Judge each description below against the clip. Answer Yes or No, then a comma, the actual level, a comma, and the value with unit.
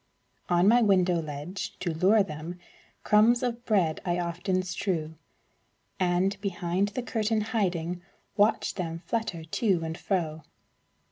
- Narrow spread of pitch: No, average, 3.6 semitones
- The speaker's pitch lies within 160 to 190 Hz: Yes, medium, 185 Hz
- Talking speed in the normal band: No, slow, 130 wpm